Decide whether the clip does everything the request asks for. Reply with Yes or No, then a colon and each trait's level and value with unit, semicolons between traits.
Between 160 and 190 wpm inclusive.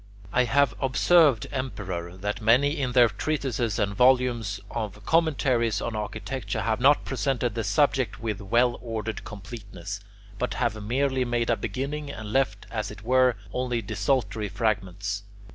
No: average, 145 wpm